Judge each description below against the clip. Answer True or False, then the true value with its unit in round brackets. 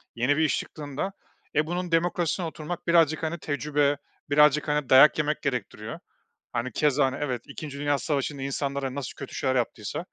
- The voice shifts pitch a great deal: False (2.6 semitones)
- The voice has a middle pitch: True (145 Hz)